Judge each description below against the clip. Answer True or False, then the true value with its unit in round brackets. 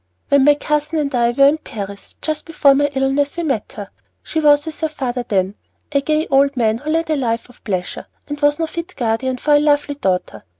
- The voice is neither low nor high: False (280 Hz)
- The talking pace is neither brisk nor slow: False (225 wpm)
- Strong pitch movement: False (3.7 semitones)